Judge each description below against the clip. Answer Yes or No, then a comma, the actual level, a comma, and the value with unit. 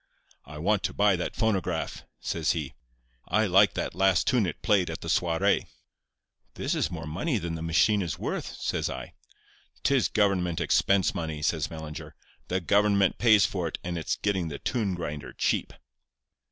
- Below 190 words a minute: Yes, average, 170 wpm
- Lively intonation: No, average, 3.7 semitones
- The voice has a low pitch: Yes, very low, 90 Hz